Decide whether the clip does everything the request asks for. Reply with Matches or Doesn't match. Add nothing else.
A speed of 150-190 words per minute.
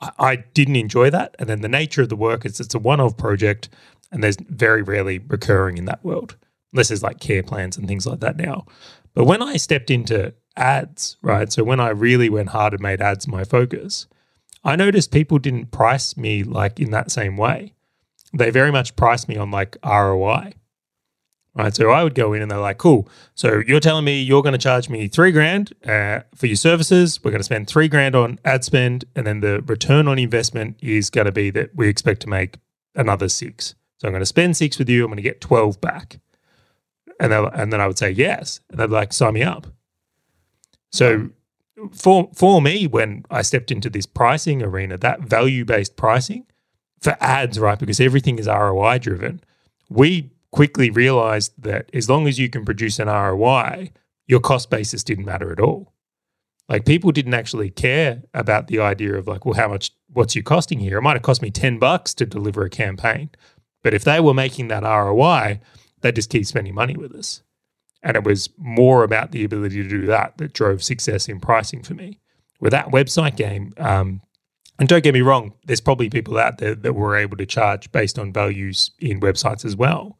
Doesn't match